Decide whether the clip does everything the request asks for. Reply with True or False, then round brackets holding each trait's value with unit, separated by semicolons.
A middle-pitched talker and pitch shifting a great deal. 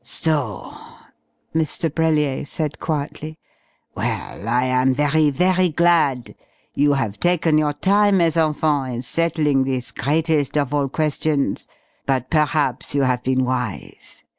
False (145 Hz; 3.3 semitones)